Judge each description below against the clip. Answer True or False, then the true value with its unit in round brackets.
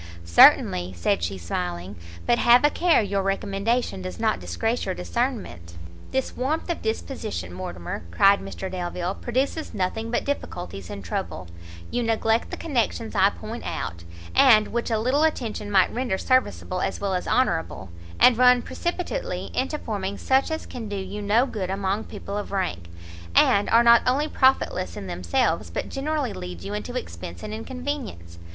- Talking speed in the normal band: True (165 wpm)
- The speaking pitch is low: False (205 Hz)